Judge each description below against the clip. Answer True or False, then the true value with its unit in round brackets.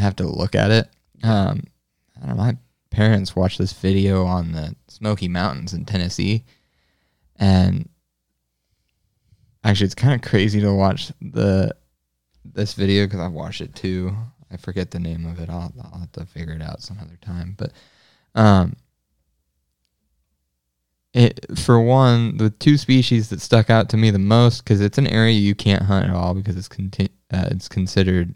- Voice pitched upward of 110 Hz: False (95 Hz)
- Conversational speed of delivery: True (175 wpm)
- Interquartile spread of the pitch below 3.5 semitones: False (4.3 semitones)